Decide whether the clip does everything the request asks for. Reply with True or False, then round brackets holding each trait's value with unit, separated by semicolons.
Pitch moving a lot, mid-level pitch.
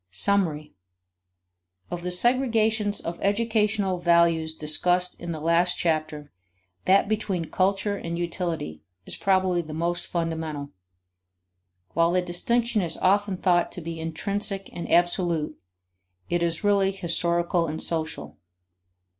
False (3.0 semitones; 175 Hz)